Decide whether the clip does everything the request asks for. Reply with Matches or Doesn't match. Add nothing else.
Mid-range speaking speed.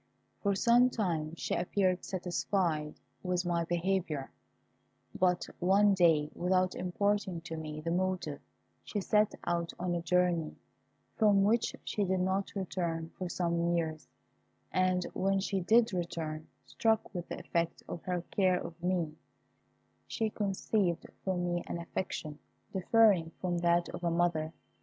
Matches